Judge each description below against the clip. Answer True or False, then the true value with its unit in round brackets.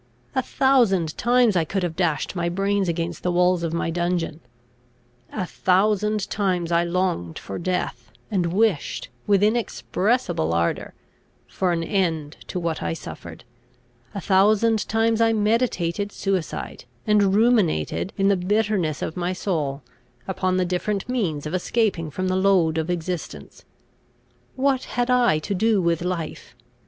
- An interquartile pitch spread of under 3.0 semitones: False (4.0 semitones)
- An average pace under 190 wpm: True (145 wpm)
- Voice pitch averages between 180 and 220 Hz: True (185 Hz)